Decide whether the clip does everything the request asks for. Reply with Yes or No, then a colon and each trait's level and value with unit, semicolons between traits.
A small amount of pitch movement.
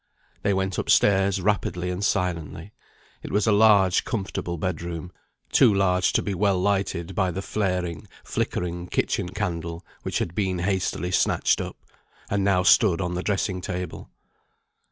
Yes: narrow, 2.0 semitones